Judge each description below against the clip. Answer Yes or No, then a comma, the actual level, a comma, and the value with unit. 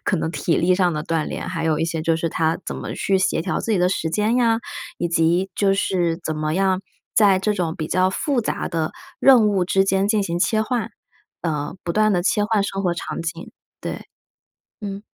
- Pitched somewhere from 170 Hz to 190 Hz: Yes, medium, 185 Hz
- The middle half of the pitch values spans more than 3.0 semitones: Yes, average, 3.6 semitones